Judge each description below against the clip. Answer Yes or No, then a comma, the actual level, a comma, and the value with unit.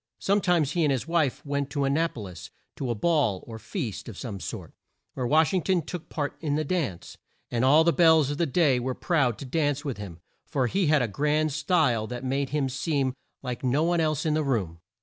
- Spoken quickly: Yes, fast, 235 wpm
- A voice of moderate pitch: Yes, medium, 145 Hz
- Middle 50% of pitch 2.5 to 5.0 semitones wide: Yes, average, 4.4 semitones